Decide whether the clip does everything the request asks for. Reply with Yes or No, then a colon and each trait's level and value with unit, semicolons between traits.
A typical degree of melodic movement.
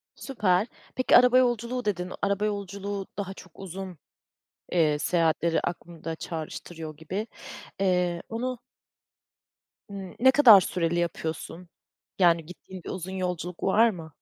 Yes: average, 3.3 semitones